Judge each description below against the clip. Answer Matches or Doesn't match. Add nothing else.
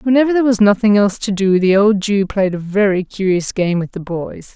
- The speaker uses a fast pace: Matches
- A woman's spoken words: Matches